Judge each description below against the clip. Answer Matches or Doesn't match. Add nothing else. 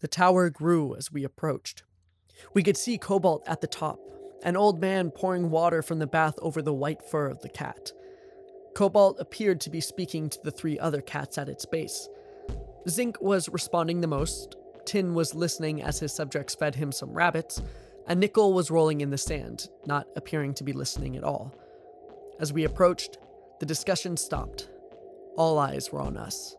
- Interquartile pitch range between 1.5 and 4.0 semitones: Doesn't match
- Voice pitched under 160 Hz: Doesn't match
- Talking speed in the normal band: Matches